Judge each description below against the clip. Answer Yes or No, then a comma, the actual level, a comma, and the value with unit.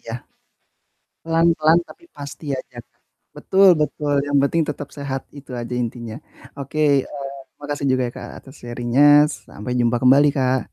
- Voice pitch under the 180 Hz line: Yes, medium, 140 Hz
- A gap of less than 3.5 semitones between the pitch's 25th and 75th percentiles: Yes, average, 2.9 semitones